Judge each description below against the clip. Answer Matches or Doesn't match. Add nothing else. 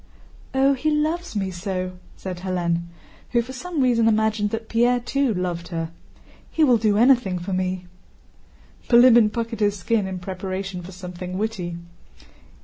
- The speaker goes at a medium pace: Matches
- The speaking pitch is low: Doesn't match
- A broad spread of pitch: Doesn't match